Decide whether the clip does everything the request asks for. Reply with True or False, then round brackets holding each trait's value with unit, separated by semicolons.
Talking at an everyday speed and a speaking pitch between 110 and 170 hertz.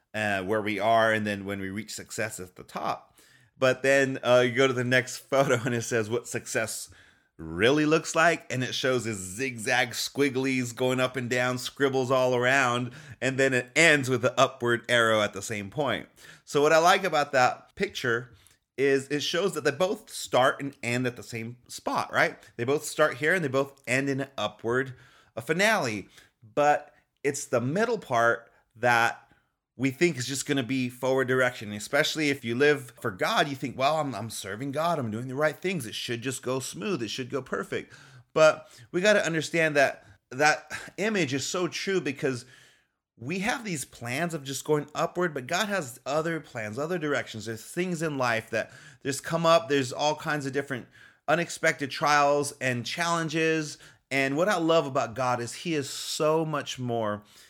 True (195 wpm; 135 Hz)